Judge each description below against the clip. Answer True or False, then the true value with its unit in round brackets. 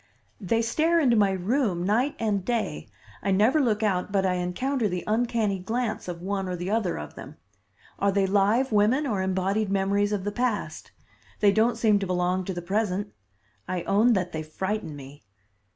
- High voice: True (200 Hz)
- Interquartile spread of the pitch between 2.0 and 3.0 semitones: False (3.4 semitones)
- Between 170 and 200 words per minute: True (185 wpm)